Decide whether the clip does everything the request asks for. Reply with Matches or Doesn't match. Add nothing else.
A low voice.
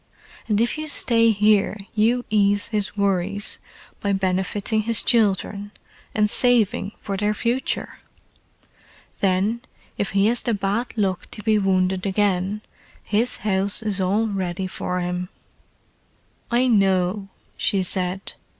Doesn't match